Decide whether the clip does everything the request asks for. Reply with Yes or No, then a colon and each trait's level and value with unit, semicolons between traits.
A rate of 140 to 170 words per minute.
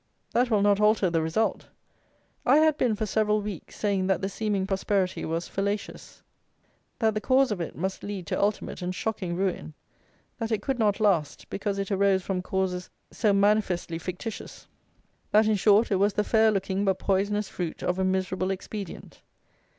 No: average, 180 wpm